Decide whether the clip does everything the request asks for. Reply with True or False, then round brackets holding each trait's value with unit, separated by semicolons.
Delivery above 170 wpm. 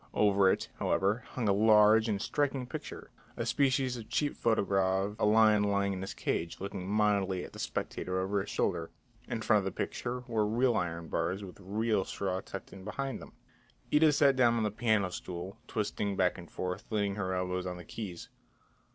True (195 wpm)